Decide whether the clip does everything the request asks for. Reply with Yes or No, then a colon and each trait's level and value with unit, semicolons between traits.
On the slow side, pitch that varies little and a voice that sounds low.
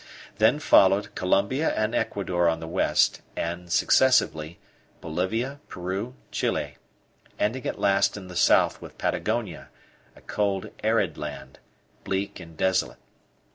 No: slow, 125 wpm; average, 3.7 semitones; very low, 95 Hz